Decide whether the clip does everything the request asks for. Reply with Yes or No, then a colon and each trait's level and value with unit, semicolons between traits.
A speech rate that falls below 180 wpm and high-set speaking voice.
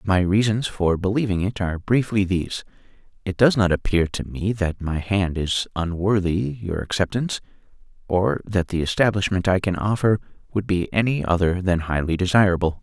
No: average, 165 wpm; very low, 95 Hz